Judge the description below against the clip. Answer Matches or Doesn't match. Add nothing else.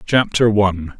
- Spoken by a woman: Doesn't match